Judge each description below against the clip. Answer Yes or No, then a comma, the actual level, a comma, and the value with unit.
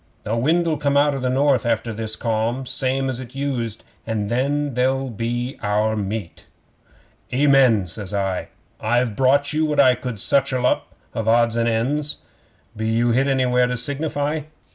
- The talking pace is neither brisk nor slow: Yes, average, 165 wpm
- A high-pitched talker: No, low, 125 Hz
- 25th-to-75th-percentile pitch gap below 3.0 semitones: No, average, 3.6 semitones